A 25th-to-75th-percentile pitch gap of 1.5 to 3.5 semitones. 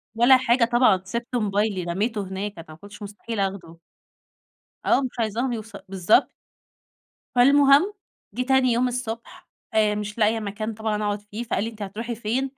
Yes: average, 2.9 semitones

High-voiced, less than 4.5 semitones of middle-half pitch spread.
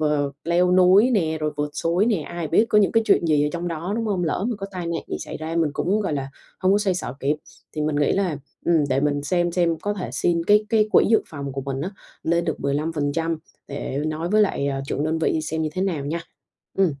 No: medium, 165 Hz; average, 3.9 semitones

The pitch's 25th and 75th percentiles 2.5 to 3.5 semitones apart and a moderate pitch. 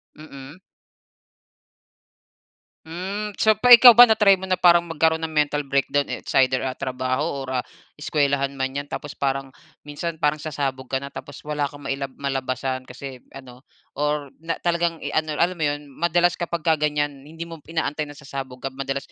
Yes: average, 3.2 semitones; medium, 145 Hz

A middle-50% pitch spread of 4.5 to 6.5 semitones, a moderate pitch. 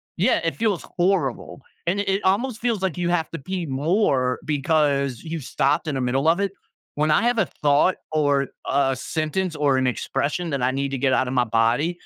Yes: average, 5.0 semitones; medium, 150 Hz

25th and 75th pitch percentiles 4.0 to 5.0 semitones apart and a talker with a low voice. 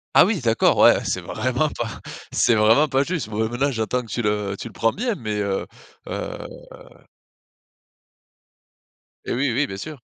Yes: average, 4.6 semitones; low, 120 Hz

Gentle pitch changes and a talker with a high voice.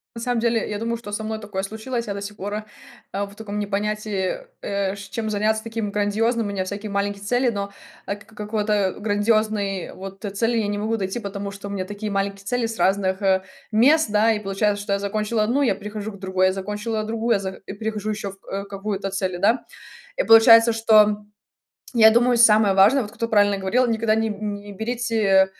Yes: narrow, 1.9 semitones; high, 210 Hz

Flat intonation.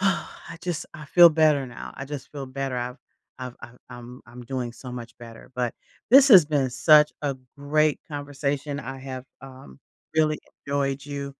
No: average, 3.1 semitones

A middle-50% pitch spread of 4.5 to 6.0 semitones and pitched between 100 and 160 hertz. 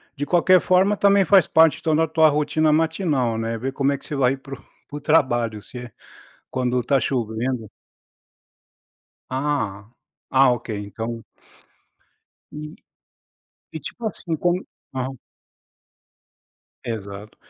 Yes: average, 5.1 semitones; low, 135 Hz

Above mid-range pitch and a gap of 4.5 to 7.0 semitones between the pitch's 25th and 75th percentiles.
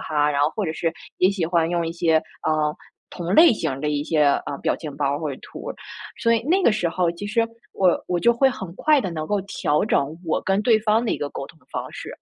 No: medium, 170 Hz; wide, 5.6 semitones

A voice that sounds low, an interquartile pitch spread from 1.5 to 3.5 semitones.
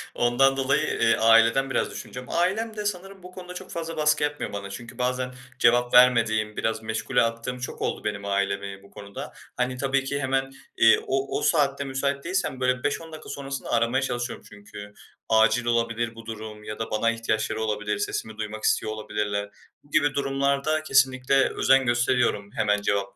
No: low, 120 Hz; average, 4.0 semitones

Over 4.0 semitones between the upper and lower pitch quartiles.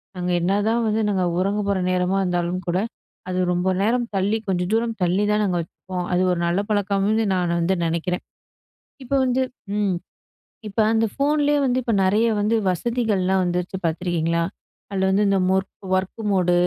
No: average, 3.2 semitones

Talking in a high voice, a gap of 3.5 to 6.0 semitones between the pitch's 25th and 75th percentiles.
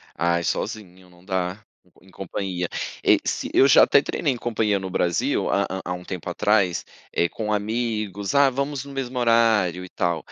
No: low, 100 Hz; average, 4.5 semitones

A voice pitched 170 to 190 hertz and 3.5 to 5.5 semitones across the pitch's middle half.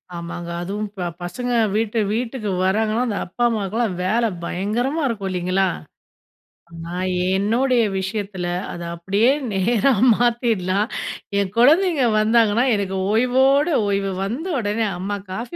No: high, 215 Hz; average, 3.9 semitones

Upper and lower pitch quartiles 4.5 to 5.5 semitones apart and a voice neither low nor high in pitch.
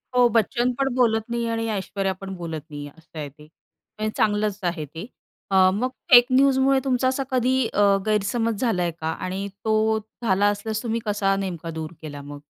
No: average, 5.2 semitones; high, 210 Hz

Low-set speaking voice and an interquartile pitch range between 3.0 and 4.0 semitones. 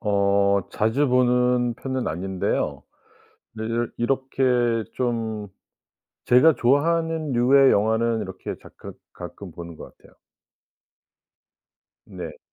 Yes: low, 120 Hz; average, 3.6 semitones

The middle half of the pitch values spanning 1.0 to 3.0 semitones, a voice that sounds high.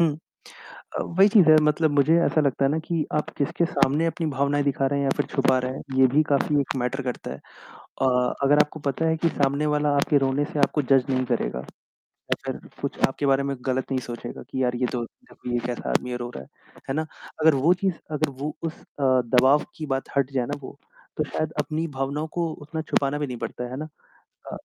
No: average, 2.7 semitones; medium, 140 Hz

